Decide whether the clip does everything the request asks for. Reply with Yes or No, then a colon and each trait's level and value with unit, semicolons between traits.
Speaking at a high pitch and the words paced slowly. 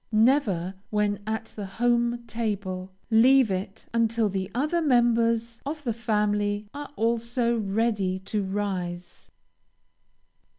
Yes: high, 220 Hz; slow, 115 wpm